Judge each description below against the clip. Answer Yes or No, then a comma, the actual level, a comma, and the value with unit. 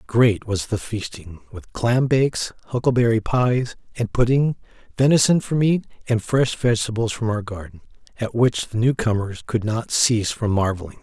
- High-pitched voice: No, low, 115 Hz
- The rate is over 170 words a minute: No, average, 160 wpm